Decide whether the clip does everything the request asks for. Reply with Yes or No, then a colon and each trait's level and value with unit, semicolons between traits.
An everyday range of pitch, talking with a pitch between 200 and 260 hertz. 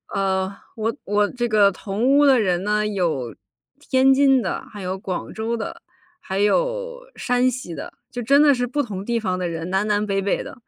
Yes: average, 4.9 semitones; high, 210 Hz